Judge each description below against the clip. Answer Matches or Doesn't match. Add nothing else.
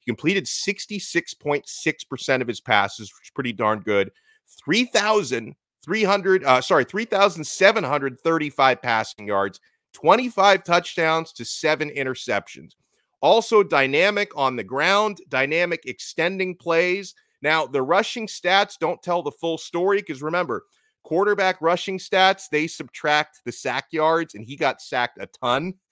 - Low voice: Doesn't match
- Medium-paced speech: Doesn't match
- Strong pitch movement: Matches